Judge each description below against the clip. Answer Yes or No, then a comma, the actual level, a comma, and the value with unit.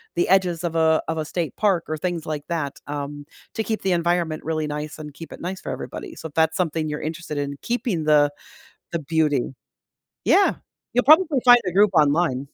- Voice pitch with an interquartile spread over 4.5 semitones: No, average, 3.0 semitones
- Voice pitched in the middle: Yes, medium, 160 Hz